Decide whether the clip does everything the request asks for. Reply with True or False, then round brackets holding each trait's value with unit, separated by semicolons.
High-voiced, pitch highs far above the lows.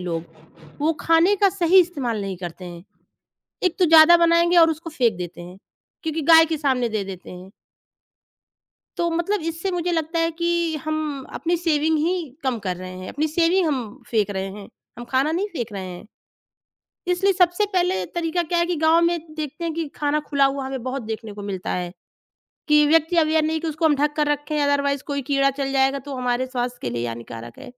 True (300 Hz; 5.7 semitones)